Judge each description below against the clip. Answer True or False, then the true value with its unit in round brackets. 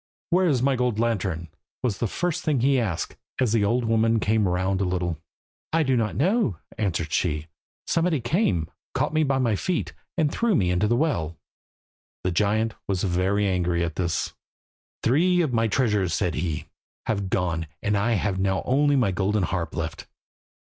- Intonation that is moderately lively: False (6.3 semitones)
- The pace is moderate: True (175 wpm)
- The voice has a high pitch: False (105 Hz)